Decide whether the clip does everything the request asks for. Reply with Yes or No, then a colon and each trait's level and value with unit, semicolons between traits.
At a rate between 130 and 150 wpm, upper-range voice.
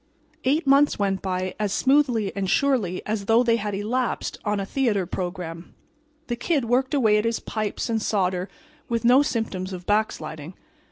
No: average, 170 wpm; high, 215 Hz